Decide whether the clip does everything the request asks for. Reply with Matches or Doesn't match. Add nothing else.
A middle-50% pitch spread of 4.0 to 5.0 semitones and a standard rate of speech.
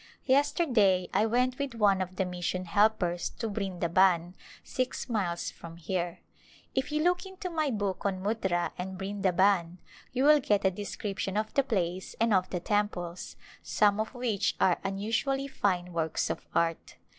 Matches